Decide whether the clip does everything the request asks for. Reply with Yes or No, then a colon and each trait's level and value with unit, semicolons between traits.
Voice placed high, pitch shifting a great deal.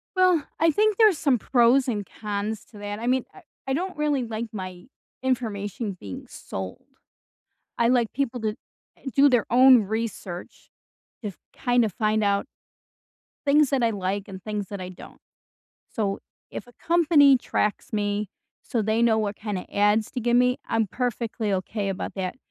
No: high, 225 Hz; average, 3.9 semitones